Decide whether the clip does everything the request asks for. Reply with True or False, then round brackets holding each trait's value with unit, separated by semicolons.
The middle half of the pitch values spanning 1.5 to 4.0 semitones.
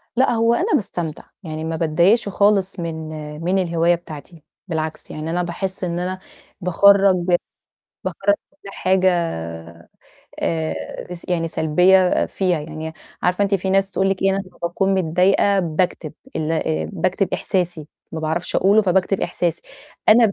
True (3.1 semitones)